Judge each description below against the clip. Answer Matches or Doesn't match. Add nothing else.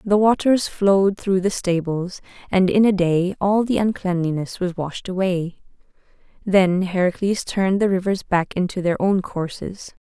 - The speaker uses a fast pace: Doesn't match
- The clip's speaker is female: Matches